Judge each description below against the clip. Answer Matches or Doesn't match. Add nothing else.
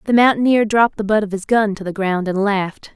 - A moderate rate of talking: Doesn't match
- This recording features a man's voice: Doesn't match